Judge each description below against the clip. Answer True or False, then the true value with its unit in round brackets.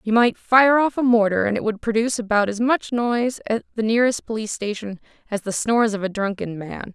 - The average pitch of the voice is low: False (220 Hz)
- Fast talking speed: True (225 wpm)